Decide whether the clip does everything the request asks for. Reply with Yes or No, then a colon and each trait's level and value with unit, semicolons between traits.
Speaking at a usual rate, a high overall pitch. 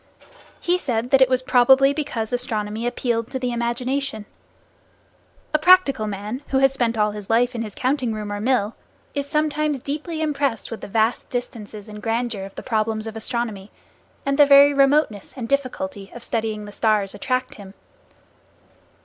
Yes: average, 170 wpm; high, 240 Hz